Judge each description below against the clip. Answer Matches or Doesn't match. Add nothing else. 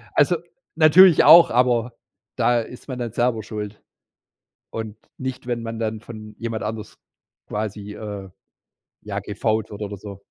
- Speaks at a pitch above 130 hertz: Doesn't match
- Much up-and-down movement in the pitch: Doesn't match